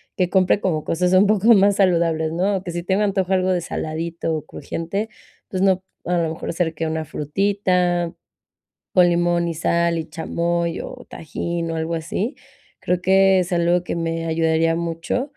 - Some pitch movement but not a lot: No, narrow, 2.3 semitones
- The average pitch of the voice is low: No, medium, 175 Hz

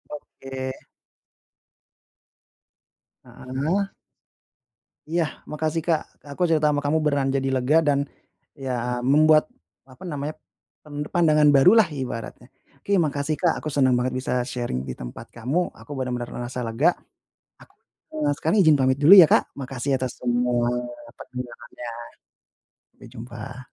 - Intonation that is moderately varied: Yes, average, 3.6 semitones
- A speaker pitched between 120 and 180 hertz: Yes, medium, 140 Hz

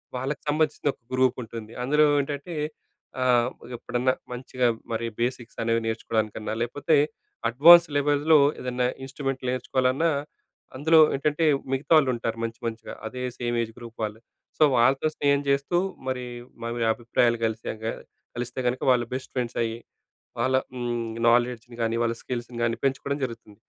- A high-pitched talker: No, low, 125 Hz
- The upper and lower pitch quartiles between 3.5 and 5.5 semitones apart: No, average, 3.0 semitones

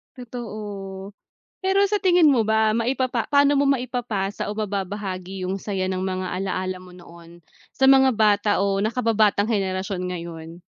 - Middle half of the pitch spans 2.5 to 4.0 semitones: No, average, 4.7 semitones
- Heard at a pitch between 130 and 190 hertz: No, high, 205 Hz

